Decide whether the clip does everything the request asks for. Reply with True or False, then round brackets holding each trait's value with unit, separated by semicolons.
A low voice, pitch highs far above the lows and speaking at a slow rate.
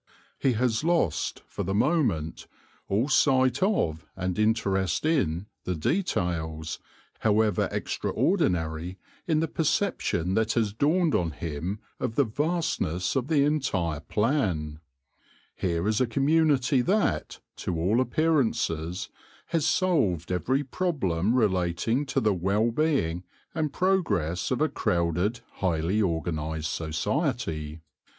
True (105 Hz; 8.9 semitones; 125 wpm)